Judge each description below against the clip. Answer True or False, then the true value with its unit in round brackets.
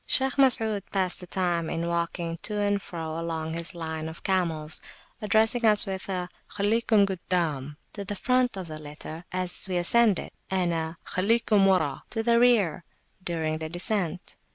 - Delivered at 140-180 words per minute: True (165 wpm)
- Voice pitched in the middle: True (180 Hz)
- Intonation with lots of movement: False (4.0 semitones)